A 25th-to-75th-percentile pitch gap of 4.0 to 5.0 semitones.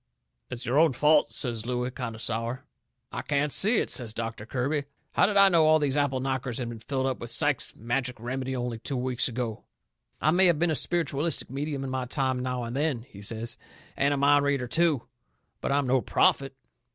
No: average, 3.2 semitones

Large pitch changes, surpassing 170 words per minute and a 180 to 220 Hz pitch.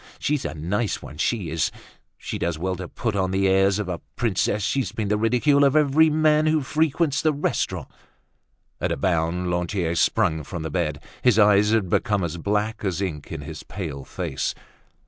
No: wide, 6.1 semitones; average, 190 wpm; low, 100 Hz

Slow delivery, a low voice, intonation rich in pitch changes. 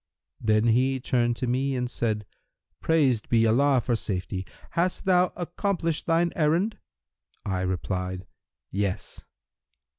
Yes: slow, 120 wpm; low, 125 Hz; wide, 7.3 semitones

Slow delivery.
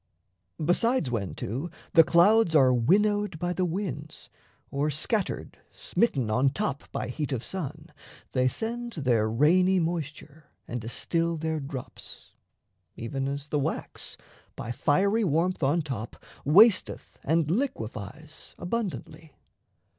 Yes: slow, 125 wpm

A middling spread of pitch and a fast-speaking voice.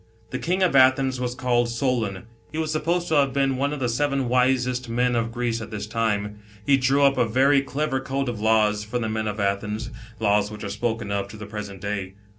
Yes: average, 4.1 semitones; fast, 230 wpm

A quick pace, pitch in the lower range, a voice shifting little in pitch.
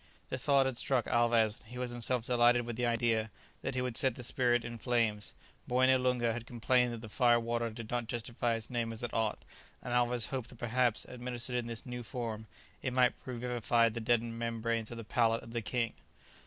Yes: fast, 215 wpm; low, 120 Hz; narrow, 1.2 semitones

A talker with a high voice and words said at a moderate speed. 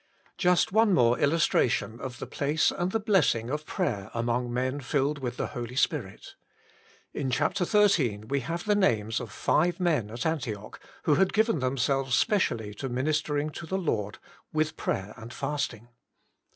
No: low, 135 Hz; average, 165 wpm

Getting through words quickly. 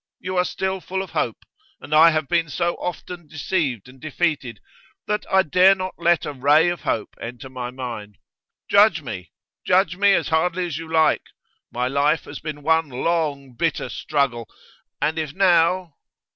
No: average, 170 wpm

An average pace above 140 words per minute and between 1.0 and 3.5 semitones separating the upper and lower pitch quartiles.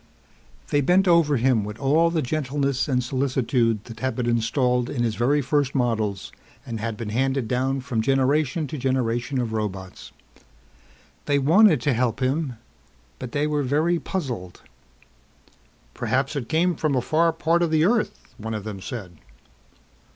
No: average, 160 wpm; average, 4.2 semitones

